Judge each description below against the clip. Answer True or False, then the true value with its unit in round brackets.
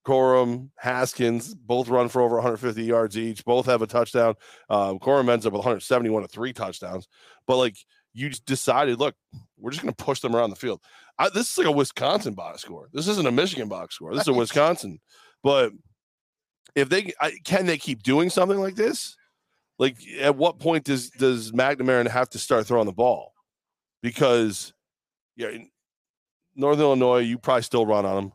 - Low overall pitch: True (125 Hz)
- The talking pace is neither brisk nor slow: True (190 wpm)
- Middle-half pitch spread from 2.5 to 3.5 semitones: True (3.0 semitones)